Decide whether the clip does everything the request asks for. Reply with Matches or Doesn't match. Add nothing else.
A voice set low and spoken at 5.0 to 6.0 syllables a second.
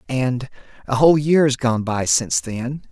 Doesn't match